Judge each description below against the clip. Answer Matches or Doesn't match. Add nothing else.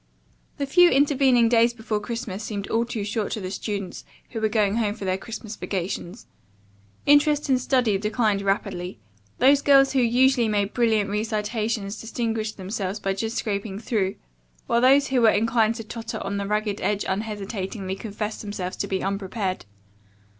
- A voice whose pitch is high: Matches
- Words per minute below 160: Doesn't match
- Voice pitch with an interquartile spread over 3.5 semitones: Doesn't match